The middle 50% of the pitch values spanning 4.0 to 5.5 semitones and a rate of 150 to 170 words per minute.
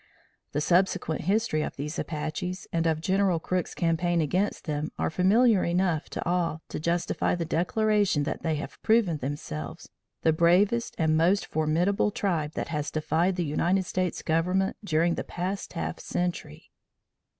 No: average, 3.1 semitones; average, 155 wpm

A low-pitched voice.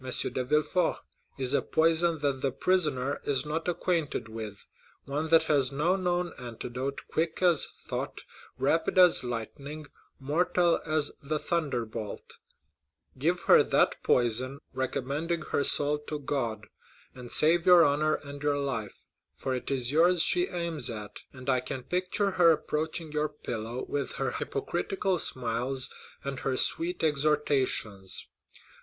No: medium, 145 Hz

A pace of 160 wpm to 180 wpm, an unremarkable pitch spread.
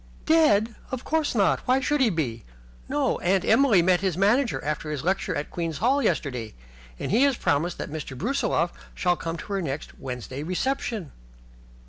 No: average, 175 wpm; wide, 8.3 semitones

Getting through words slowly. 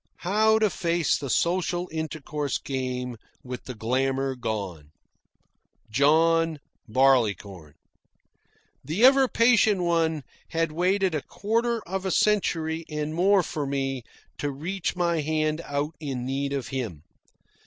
Yes: slow, 125 wpm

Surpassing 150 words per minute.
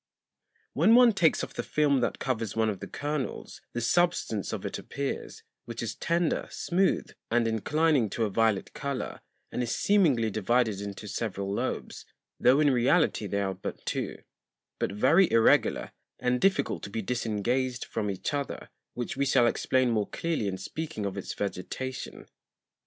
Yes: average, 165 wpm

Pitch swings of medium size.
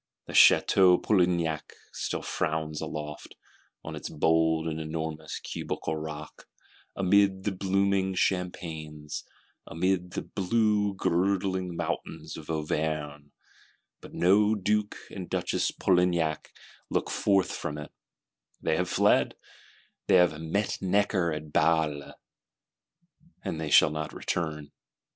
Yes: average, 3.6 semitones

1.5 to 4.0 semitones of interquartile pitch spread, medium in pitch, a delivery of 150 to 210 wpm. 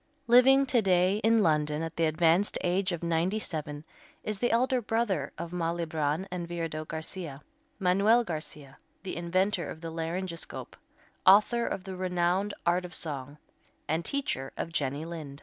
Yes: average, 3.6 semitones; medium, 175 Hz; average, 155 wpm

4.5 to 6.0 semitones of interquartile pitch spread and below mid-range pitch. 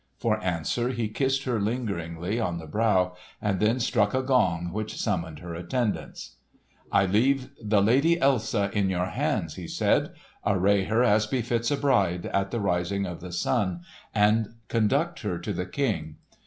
Yes: average, 4.8 semitones; low, 105 Hz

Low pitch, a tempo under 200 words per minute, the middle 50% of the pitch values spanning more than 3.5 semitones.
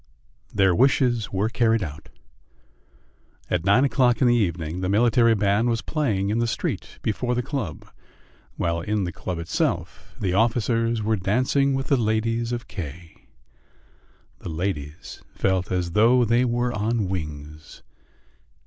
Yes: low, 110 Hz; average, 145 wpm; average, 4.6 semitones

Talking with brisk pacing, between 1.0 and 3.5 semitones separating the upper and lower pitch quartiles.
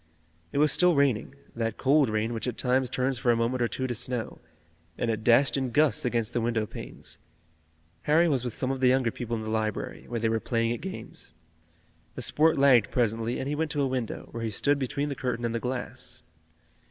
Yes: fast, 225 wpm; average, 2.9 semitones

